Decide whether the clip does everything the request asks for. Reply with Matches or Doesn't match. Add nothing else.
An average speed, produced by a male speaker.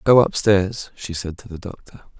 Matches